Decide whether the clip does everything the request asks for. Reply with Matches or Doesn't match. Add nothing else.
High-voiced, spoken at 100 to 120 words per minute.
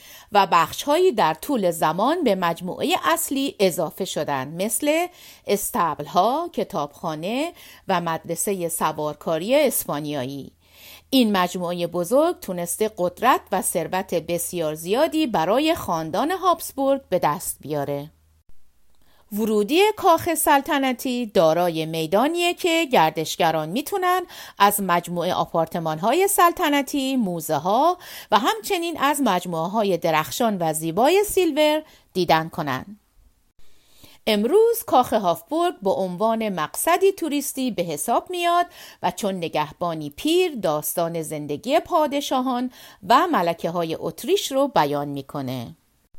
Matches